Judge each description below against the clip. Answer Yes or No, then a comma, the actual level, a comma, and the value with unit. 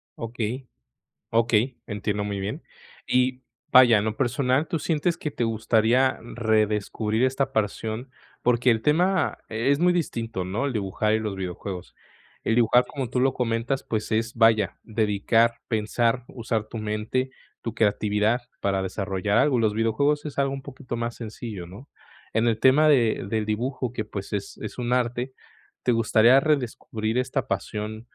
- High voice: No, low, 115 Hz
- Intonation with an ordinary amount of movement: Yes, average, 3.1 semitones